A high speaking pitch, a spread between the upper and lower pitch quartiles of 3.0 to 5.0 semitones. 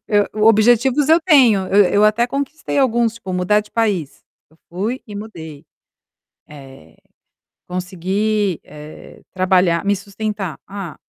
Yes: high, 205 Hz; average, 3.8 semitones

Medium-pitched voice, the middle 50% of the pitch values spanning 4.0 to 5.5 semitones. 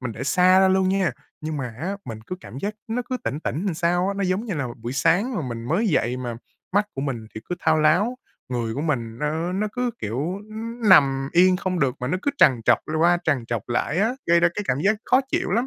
No: medium, 165 Hz; wide, 6.7 semitones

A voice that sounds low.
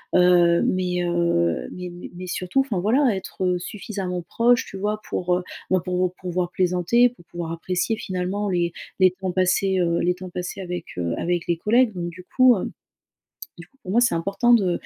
No: medium, 180 Hz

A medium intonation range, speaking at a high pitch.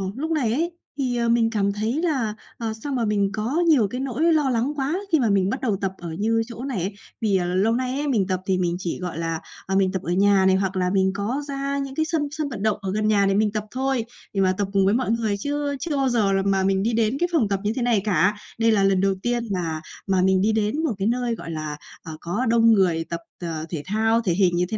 Yes: average, 4.8 semitones; high, 215 Hz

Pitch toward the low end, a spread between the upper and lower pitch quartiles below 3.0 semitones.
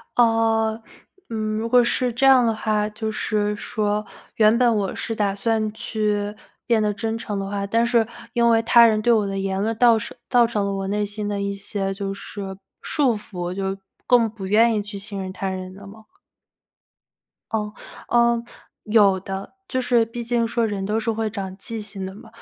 No: high, 215 Hz; narrow, 2.4 semitones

